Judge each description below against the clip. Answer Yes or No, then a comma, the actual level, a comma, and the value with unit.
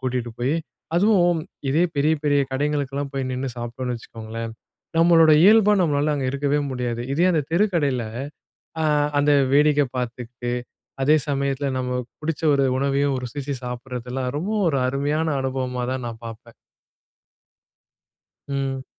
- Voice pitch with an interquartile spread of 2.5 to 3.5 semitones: Yes, average, 2.9 semitones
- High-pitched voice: No, low, 135 Hz